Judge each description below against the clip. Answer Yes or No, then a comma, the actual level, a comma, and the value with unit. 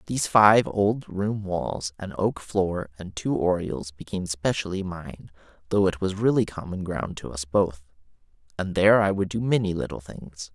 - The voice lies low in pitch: Yes, very low, 90 Hz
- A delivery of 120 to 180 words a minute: Yes, average, 175 wpm